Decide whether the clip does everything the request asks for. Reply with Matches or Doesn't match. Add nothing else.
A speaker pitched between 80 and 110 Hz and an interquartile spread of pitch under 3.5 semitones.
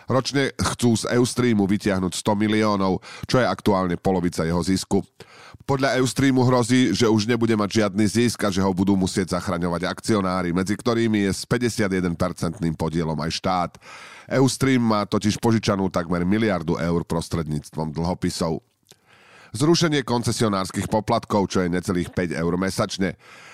Doesn't match